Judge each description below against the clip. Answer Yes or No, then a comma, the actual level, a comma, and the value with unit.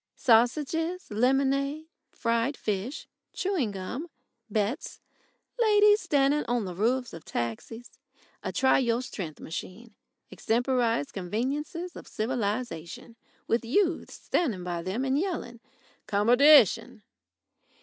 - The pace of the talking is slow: Yes, slow, 105 wpm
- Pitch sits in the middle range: No, high, 245 Hz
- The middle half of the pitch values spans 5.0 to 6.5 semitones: Yes, average, 5.3 semitones